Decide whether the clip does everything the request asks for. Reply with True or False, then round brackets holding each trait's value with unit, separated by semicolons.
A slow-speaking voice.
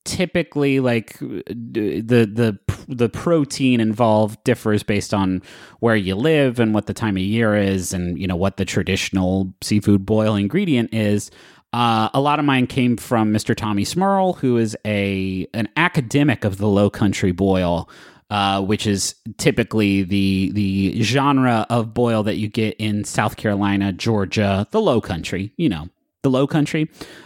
False (165 wpm)